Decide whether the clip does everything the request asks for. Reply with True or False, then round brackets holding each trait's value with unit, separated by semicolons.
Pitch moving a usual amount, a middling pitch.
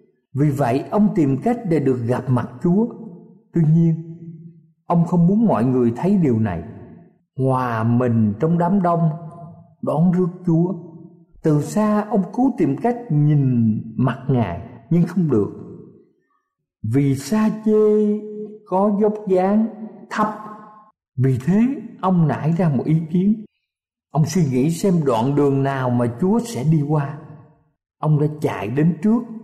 False (6.9 semitones; 170 Hz)